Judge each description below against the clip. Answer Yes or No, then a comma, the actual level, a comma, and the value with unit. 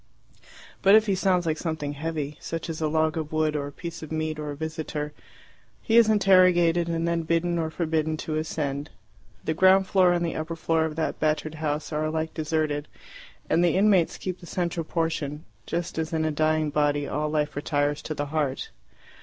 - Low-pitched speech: No, medium, 160 Hz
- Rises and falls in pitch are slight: Yes, narrow, 1.9 semitones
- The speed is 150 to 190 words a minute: No, average, 200 wpm